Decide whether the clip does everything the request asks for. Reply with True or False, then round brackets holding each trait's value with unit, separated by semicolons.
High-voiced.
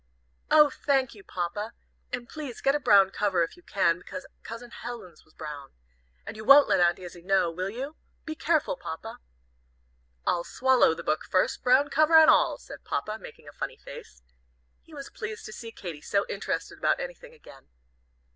True (220 Hz)